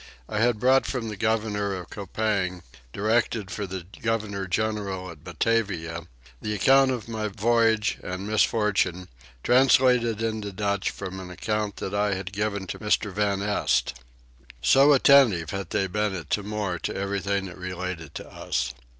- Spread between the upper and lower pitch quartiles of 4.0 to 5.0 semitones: No, average, 2.8 semitones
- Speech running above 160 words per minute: No, average, 155 wpm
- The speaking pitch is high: No, low, 105 Hz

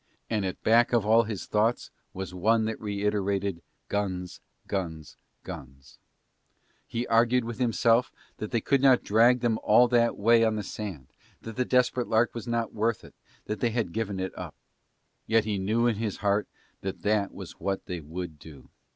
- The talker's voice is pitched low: Yes, low, 110 Hz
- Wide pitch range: No, average, 3.2 semitones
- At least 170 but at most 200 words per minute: Yes, average, 180 wpm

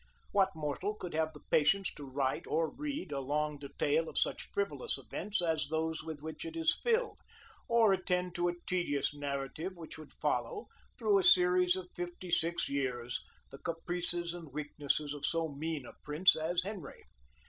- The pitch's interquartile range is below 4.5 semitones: Yes, average, 3.7 semitones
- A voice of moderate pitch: Yes, medium, 165 Hz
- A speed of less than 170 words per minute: No, average, 175 wpm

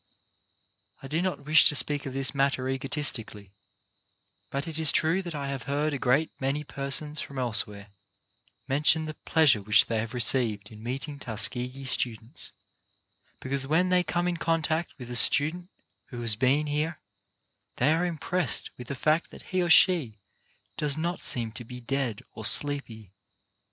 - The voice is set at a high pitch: No, medium, 140 Hz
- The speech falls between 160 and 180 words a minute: Yes, average, 170 wpm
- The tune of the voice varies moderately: Yes, average, 4.3 semitones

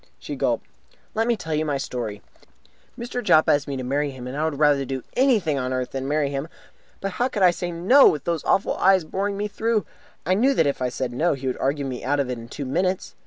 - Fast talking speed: Yes, fast, 260 wpm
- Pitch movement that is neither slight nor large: No, wide, 6.1 semitones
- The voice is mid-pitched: Yes, medium, 150 Hz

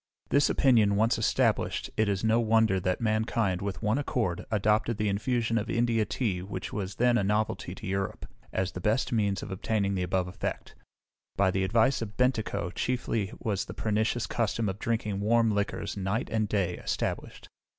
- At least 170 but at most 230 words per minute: Yes, average, 180 wpm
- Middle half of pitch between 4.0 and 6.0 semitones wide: No, average, 2.8 semitones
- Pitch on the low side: Yes, low, 105 Hz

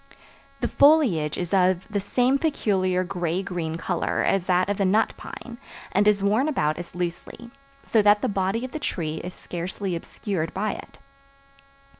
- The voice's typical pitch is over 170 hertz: Yes, high, 190 Hz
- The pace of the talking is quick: No, average, 170 wpm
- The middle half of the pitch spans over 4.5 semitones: No, average, 3.4 semitones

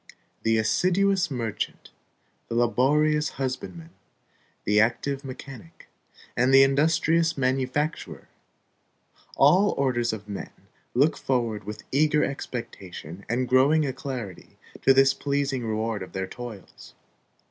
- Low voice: Yes, low, 130 Hz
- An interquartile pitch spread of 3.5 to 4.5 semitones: Yes, average, 4.2 semitones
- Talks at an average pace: No, slow, 110 wpm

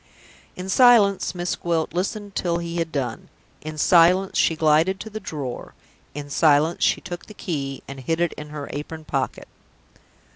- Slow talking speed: No, average, 170 wpm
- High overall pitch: No, medium, 165 Hz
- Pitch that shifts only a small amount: No, average, 3.6 semitones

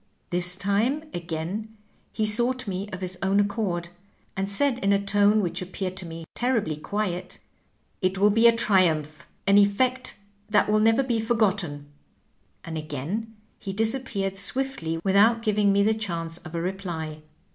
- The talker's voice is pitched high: Yes, high, 200 Hz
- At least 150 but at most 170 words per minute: Yes, average, 165 wpm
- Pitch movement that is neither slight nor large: Yes, average, 3.8 semitones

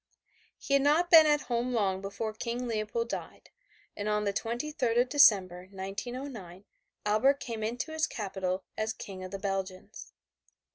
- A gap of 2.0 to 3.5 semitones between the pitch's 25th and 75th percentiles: No, average, 4.2 semitones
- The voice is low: No, high, 220 Hz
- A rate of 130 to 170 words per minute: Yes, average, 155 wpm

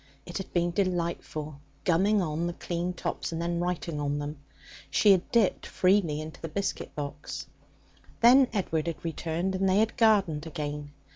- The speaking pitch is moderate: Yes, medium, 170 Hz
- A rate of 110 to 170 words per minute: Yes, average, 165 wpm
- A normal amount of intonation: Yes, average, 3.7 semitones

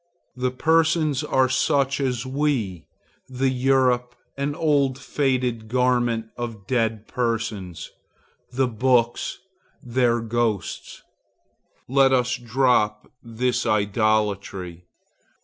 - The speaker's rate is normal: No, slow, 95 wpm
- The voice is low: Yes, low, 125 Hz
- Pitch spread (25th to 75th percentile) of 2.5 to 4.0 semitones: Yes, average, 2.8 semitones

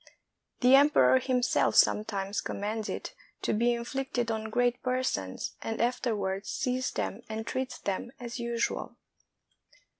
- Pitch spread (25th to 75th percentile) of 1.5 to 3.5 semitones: Yes, narrow, 2.6 semitones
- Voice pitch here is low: No, high, 235 Hz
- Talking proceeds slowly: Yes, slow, 130 wpm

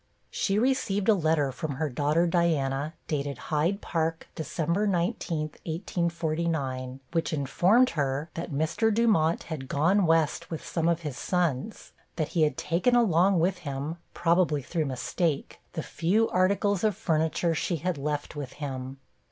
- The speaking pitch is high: No, medium, 165 Hz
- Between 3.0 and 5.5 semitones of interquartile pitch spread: Yes, average, 3.5 semitones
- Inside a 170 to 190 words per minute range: No, average, 150 wpm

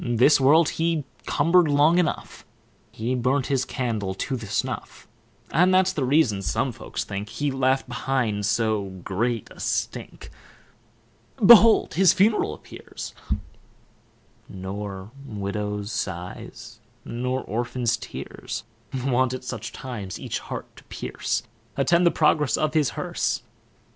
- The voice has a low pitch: Yes, low, 125 Hz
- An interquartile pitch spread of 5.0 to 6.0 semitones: Yes, wide, 5.6 semitones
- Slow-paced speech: Yes, slow, 130 wpm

